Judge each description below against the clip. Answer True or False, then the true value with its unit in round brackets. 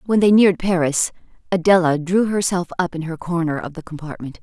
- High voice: False (175 Hz)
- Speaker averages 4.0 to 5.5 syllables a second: False (5.8 syllables/s)